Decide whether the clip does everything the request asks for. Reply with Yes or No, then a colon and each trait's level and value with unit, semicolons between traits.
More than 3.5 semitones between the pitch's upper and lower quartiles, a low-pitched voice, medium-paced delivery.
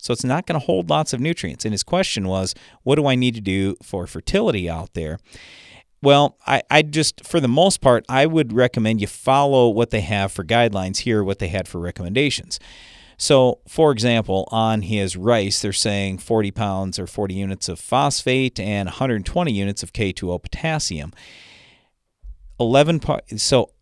Yes: average, 5.3 semitones; low, 110 Hz; average, 180 wpm